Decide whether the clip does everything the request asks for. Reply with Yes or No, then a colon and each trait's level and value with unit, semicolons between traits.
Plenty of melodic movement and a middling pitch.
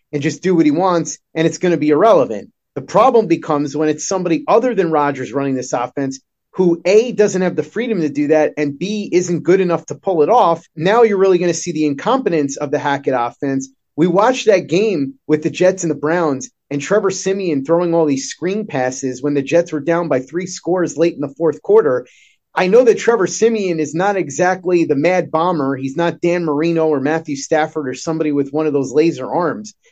No: average, 3.7 semitones; medium, 165 Hz